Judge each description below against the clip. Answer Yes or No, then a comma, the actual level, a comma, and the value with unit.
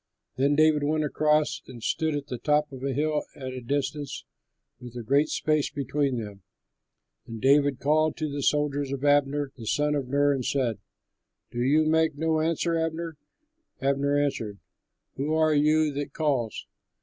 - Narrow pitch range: Yes, narrow, 2.3 semitones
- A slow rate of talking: No, average, 175 wpm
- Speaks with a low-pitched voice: No, medium, 145 Hz